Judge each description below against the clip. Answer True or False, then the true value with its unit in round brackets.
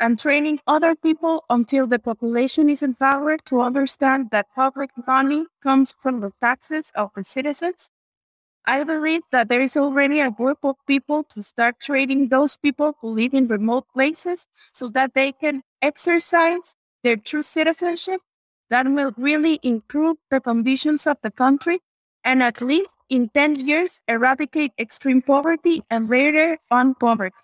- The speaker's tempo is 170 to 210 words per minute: False (155 wpm)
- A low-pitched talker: False (275 Hz)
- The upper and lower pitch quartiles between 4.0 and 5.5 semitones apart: False (3.5 semitones)